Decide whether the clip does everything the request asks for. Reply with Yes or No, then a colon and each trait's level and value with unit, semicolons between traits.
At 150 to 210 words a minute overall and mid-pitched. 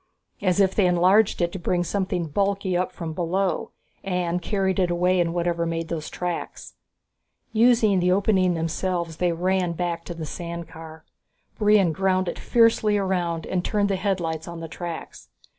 Yes: average, 175 wpm; medium, 180 Hz